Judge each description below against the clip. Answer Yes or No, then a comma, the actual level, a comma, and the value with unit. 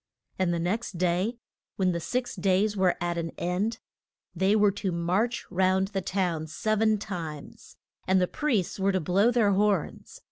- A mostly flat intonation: No, average, 3.0 semitones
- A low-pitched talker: No, high, 190 Hz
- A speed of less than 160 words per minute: No, average, 175 wpm